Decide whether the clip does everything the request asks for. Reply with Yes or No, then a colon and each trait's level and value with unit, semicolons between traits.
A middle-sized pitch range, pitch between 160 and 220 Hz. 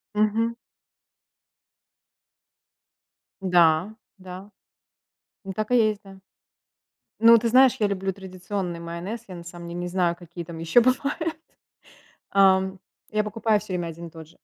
Yes: average, 3.7 semitones; high, 190 Hz